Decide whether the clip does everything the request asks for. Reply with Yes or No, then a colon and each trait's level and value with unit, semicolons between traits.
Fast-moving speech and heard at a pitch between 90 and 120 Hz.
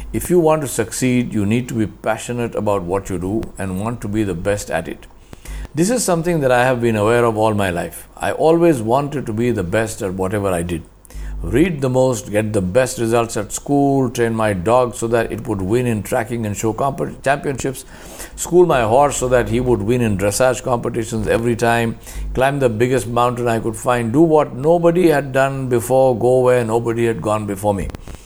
Yes: fast, 215 wpm; low, 115 Hz